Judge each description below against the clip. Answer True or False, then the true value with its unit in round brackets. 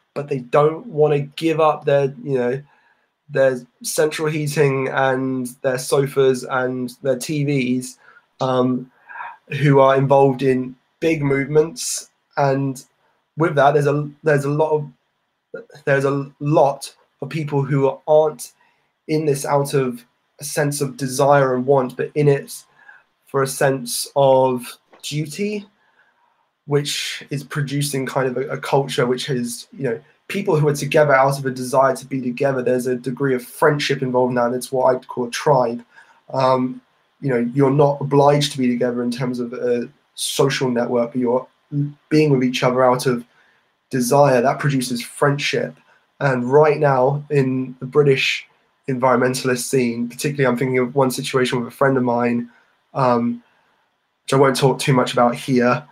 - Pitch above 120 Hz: True (135 Hz)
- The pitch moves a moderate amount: False (2.3 semitones)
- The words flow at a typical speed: True (165 wpm)